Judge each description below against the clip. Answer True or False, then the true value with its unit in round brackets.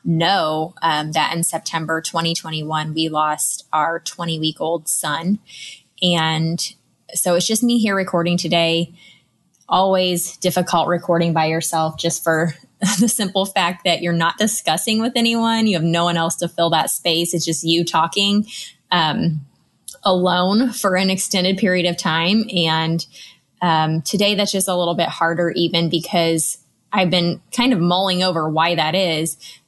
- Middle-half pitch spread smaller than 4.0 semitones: True (2.6 semitones)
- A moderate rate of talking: True (160 wpm)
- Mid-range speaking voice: True (170 Hz)